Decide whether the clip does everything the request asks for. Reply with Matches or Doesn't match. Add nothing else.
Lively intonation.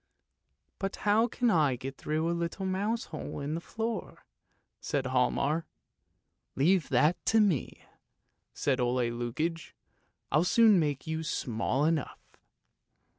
Matches